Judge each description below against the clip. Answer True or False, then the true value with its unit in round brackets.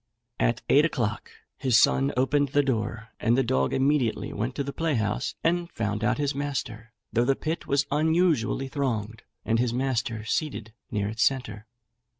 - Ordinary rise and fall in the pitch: True (4.2 semitones)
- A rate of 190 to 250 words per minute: False (165 wpm)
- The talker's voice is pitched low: True (125 Hz)